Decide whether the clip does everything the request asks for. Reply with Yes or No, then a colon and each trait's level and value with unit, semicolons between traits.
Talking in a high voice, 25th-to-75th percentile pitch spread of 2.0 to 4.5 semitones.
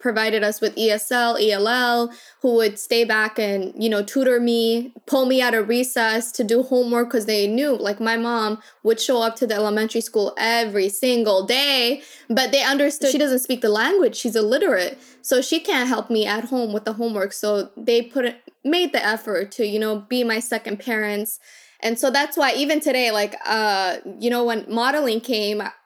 Yes: high, 235 Hz; average, 2.8 semitones